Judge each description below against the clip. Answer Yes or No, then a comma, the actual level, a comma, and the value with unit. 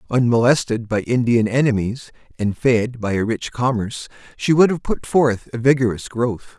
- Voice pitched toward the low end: Yes, low, 120 Hz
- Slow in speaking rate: No, average, 165 wpm